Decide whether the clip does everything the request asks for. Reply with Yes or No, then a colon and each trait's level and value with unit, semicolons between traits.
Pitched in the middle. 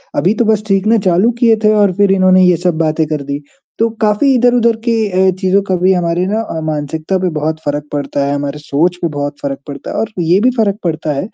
Yes: medium, 180 Hz